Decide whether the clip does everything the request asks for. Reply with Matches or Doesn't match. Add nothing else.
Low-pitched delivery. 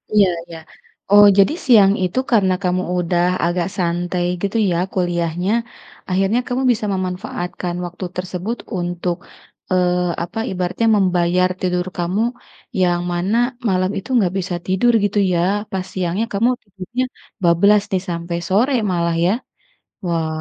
Doesn't match